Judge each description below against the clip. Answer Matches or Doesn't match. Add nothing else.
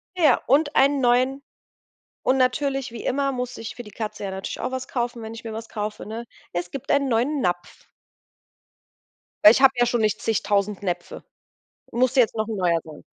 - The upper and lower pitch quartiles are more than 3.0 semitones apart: Matches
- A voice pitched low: Doesn't match